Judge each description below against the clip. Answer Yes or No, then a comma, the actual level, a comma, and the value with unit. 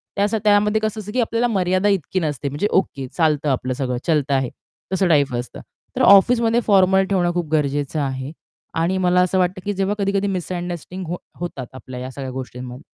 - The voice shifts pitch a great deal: Yes, wide, 5.9 semitones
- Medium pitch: Yes, medium, 175 Hz